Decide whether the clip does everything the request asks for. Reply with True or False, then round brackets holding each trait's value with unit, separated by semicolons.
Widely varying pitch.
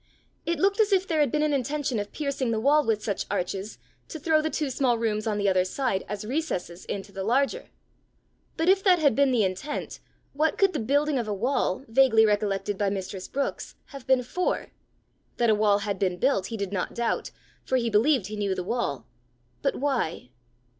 True (6.1 semitones)